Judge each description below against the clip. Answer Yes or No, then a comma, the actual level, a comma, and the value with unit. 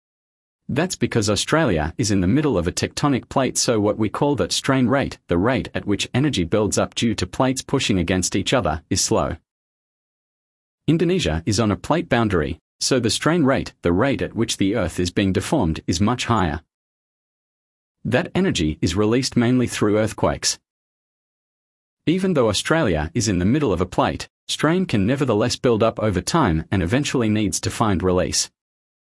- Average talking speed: Yes, average, 175 wpm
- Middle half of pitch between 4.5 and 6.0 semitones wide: Yes, average, 5.0 semitones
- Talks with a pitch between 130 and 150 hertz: No, low, 110 Hz